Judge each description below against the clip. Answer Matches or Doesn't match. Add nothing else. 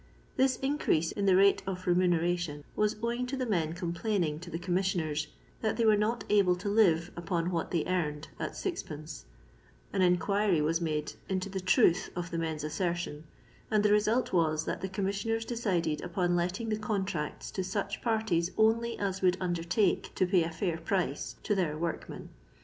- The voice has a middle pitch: Matches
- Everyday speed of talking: Matches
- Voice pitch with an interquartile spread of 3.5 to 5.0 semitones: Matches